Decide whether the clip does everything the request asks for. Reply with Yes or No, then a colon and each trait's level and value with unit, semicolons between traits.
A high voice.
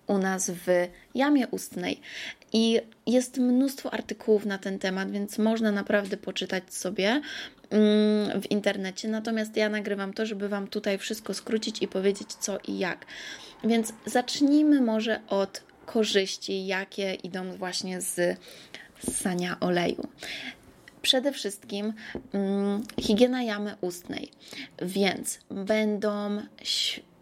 Yes: high, 210 Hz